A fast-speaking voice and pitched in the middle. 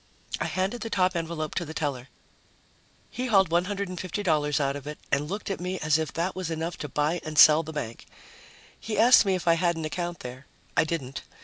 Yes: fast, 210 wpm; medium, 165 Hz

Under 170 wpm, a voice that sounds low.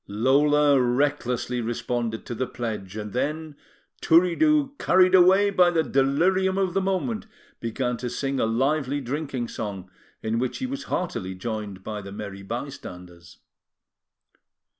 Yes: average, 140 wpm; low, 130 Hz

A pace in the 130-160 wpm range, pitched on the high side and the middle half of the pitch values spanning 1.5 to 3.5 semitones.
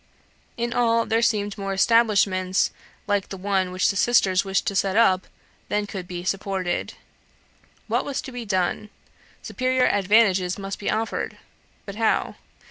Yes: average, 150 wpm; high, 200 Hz; average, 3.2 semitones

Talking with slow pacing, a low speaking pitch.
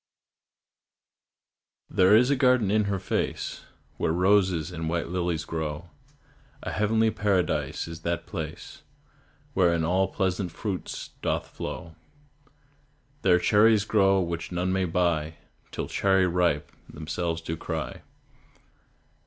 Yes: slow, 120 wpm; very low, 90 Hz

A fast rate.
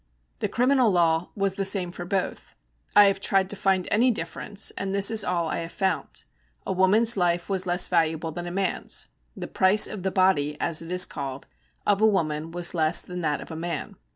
Yes: fast, 210 wpm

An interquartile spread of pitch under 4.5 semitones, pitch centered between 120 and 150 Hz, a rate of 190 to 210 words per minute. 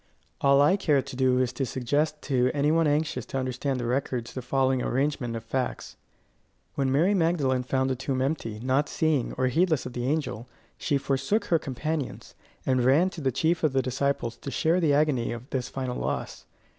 Yes: average, 2.9 semitones; low, 135 Hz; average, 195 wpm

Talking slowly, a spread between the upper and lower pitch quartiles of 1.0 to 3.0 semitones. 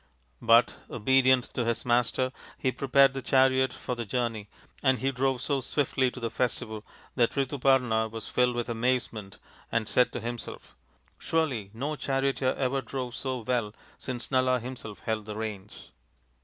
No: average, 160 wpm; narrow, 2.5 semitones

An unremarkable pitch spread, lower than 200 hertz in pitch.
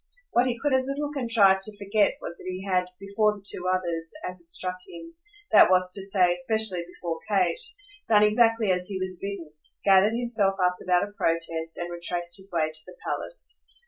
Yes: average, 3.1 semitones; high, 190 Hz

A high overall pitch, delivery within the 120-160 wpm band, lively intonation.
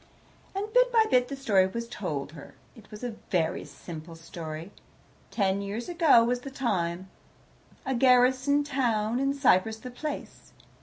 Yes: high, 235 Hz; average, 155 wpm; wide, 6.3 semitones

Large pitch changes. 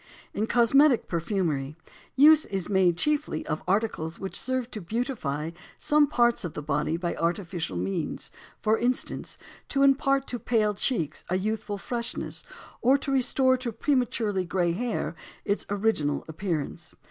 Yes: wide, 6.9 semitones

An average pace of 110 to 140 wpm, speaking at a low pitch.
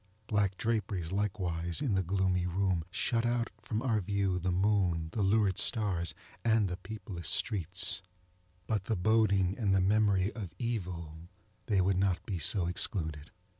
No: average, 150 wpm; very low, 95 Hz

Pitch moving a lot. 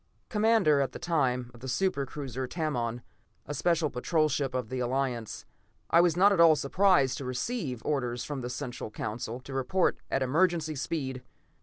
No: average, 4.9 semitones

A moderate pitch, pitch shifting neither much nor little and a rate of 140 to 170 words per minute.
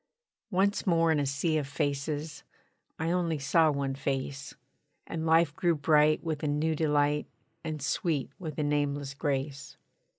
No: medium, 150 Hz; narrow, 2.3 semitones; average, 155 wpm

